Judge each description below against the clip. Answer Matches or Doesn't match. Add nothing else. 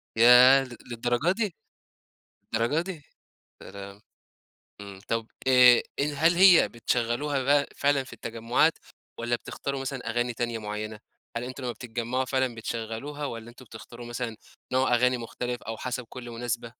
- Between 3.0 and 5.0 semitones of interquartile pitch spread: Doesn't match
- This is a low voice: Matches